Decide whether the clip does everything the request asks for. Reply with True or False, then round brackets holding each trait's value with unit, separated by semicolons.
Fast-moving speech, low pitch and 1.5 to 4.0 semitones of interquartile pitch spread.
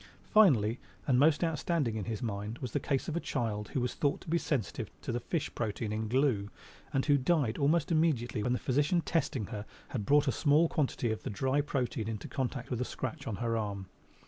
False (220 wpm; 125 Hz; 4.8 semitones)